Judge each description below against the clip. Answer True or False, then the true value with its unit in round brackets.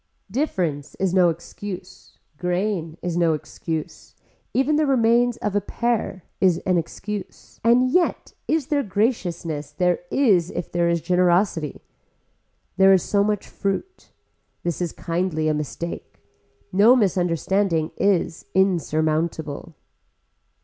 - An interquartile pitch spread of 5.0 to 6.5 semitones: False (4.0 semitones)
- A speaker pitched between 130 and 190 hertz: True (185 Hz)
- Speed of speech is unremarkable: False (120 wpm)